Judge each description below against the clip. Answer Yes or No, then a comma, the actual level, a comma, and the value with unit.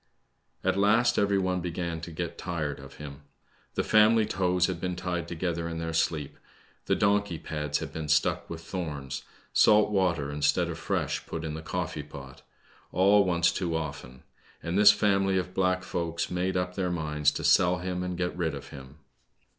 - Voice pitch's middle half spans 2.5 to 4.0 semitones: Yes, average, 2.9 semitones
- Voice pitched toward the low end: Yes, very low, 85 Hz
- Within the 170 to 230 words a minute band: Yes, average, 185 wpm